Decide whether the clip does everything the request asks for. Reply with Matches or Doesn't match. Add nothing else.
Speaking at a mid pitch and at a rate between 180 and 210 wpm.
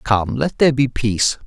Doesn't match